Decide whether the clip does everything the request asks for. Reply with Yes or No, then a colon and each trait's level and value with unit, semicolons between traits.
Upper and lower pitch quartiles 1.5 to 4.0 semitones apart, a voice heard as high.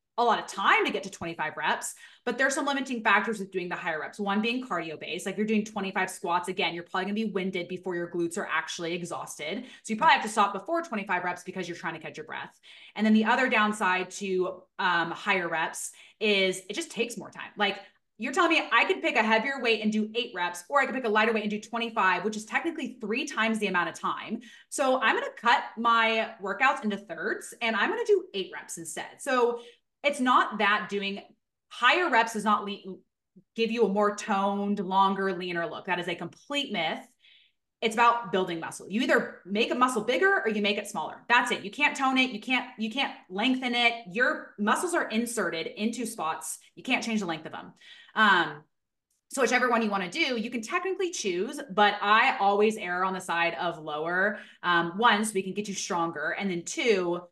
No: average, 4.4 semitones; high, 210 Hz